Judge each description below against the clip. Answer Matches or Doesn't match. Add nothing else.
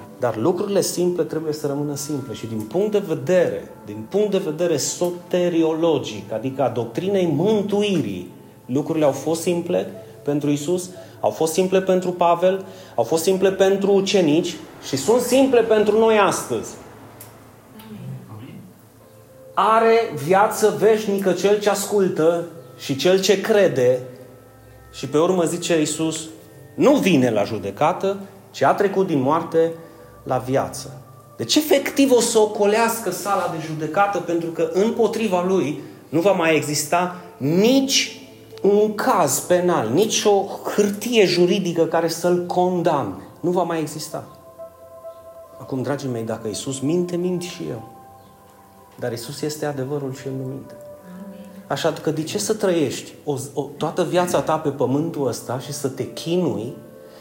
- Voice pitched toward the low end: Doesn't match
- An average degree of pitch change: Doesn't match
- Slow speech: Doesn't match